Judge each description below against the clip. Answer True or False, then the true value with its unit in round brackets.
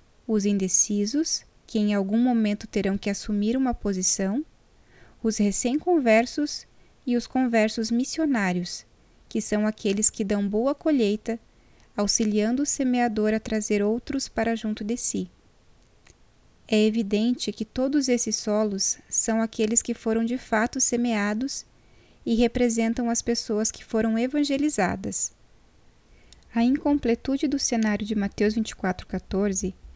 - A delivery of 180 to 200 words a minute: False (120 wpm)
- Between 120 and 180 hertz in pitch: False (225 Hz)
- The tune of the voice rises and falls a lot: False (2.7 semitones)